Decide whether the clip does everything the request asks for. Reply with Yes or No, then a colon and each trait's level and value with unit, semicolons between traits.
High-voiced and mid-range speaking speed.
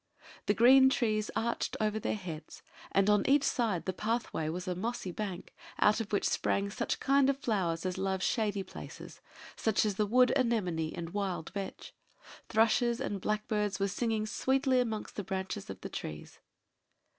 Yes: high, 210 Hz; average, 170 wpm